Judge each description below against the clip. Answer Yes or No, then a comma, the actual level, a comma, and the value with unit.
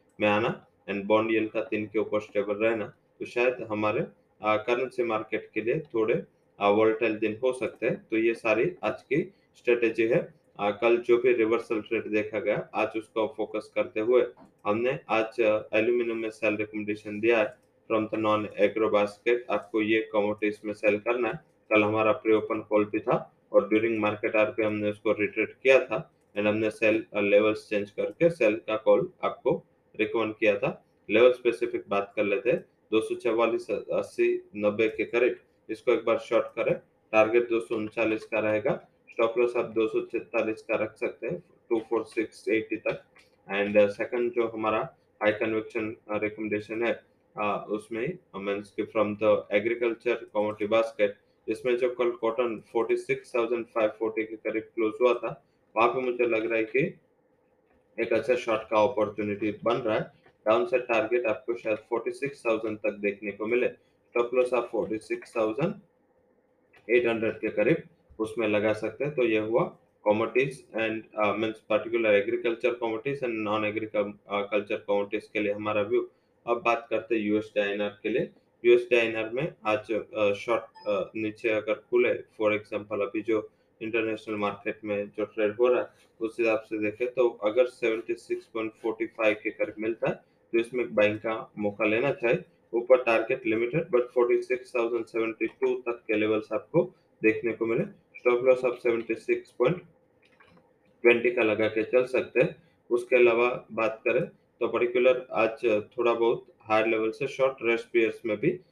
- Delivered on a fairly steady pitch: Yes, narrow, 2.2 semitones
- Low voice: Yes, low, 110 Hz